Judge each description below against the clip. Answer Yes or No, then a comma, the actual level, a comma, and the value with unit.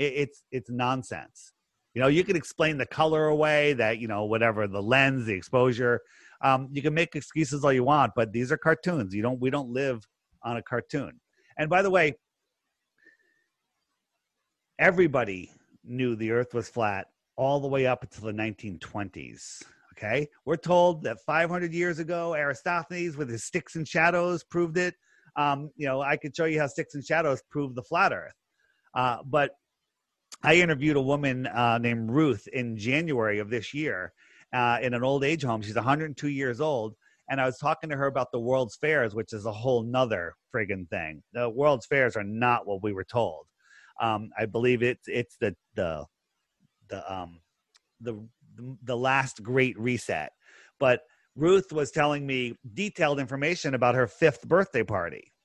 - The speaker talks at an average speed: Yes, average, 175 wpm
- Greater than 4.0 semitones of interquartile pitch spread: Yes, average, 4.5 semitones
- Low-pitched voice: Yes, low, 130 Hz